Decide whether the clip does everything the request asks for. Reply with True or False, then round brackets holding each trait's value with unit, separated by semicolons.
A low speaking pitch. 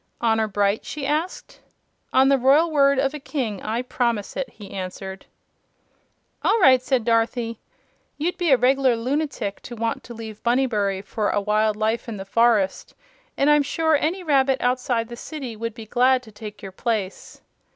False (240 Hz)